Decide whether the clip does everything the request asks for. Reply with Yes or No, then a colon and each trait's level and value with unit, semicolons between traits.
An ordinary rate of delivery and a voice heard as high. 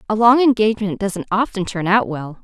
Yes: average, 195 wpm; high, 205 Hz